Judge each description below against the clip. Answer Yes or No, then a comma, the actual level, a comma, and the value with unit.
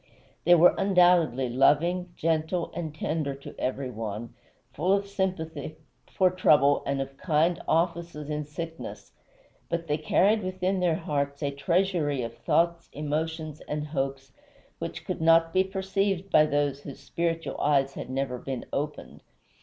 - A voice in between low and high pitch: Yes, medium, 160 Hz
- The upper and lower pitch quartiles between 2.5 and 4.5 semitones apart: Yes, average, 3.8 semitones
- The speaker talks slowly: No, average, 145 wpm